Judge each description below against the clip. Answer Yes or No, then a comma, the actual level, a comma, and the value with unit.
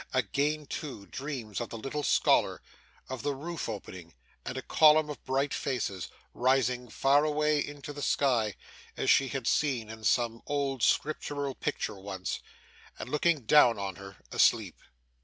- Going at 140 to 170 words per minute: Yes, average, 155 wpm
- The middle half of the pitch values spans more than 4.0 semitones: Yes, average, 4.7 semitones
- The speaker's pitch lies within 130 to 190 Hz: Yes, low, 135 Hz